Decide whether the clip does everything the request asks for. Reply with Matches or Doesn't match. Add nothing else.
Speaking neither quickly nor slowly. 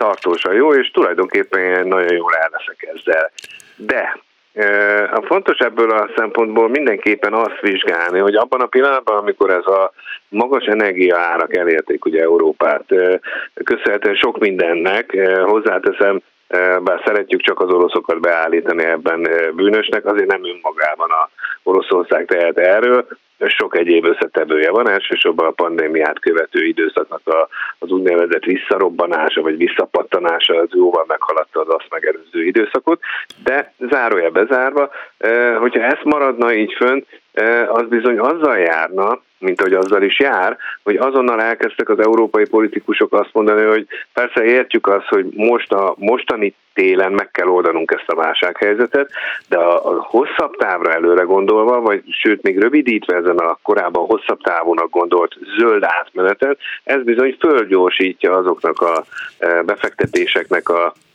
Matches